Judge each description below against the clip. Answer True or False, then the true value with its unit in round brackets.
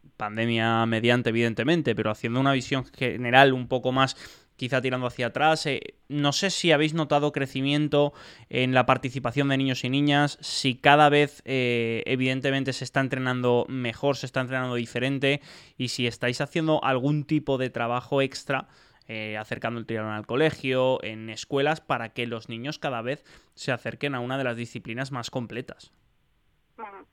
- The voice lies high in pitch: False (130 Hz)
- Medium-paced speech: True (165 wpm)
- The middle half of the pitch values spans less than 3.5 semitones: True (2.9 semitones)